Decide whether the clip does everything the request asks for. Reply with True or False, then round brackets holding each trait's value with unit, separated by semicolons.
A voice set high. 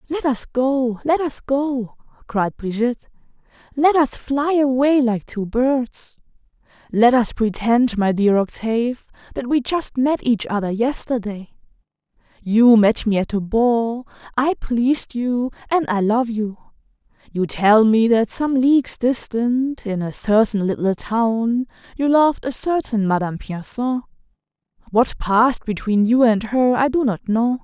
True (240 Hz)